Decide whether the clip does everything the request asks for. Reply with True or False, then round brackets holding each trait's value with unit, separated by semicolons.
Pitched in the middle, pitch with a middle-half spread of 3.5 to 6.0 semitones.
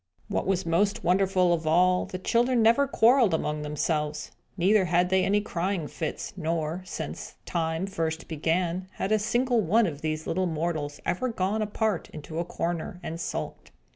True (180 Hz; 3.8 semitones)